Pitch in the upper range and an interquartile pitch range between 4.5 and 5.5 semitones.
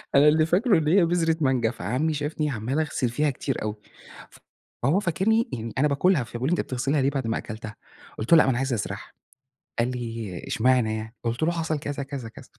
No: low, 135 Hz; average, 5.1 semitones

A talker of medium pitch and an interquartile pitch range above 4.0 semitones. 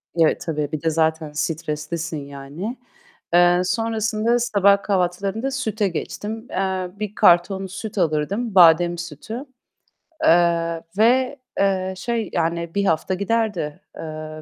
Yes: medium, 180 Hz; average, 4.6 semitones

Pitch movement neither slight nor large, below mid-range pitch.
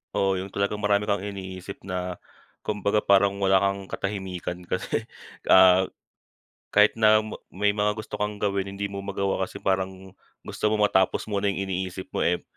No: narrow, 1.5 semitones; low, 100 Hz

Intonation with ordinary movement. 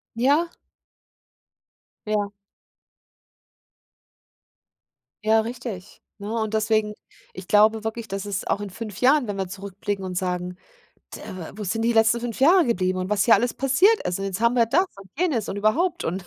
Yes: average, 3.3 semitones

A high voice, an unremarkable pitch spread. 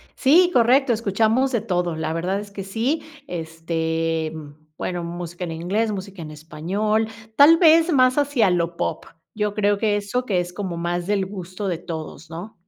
Yes: high, 195 Hz; average, 4.7 semitones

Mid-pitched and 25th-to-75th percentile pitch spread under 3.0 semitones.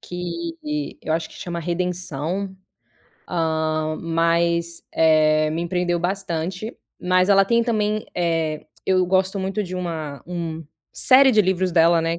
Yes: medium, 175 Hz; narrow, 2.6 semitones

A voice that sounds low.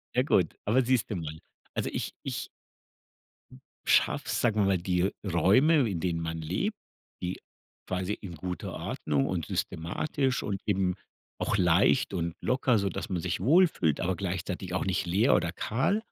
Yes: very low, 95 Hz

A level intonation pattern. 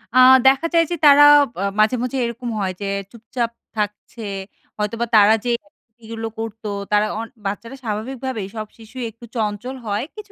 No: average, 3.0 semitones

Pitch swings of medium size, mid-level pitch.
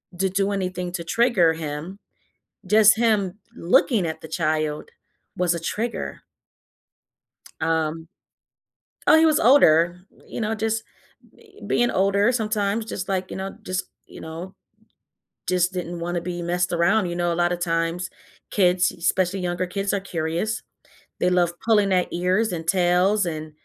Yes: average, 3.1 semitones; medium, 180 Hz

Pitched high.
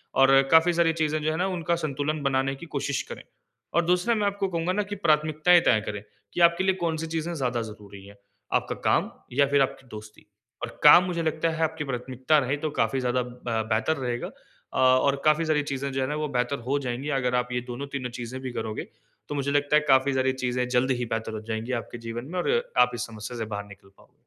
No: low, 135 Hz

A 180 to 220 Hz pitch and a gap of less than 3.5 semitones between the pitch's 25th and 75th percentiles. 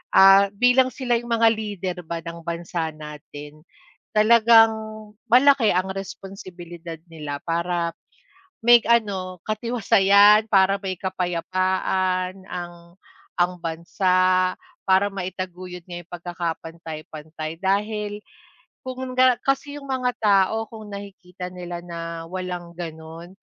No: medium, 185 Hz; average, 3.8 semitones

